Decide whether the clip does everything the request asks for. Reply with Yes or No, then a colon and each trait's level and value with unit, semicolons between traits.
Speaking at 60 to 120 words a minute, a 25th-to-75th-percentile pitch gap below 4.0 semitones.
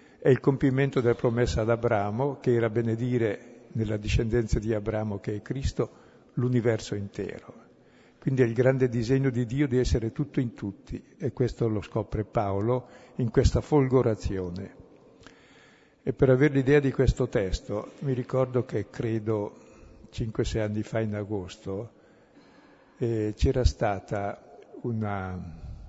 No: average, 135 wpm; average, 3.4 semitones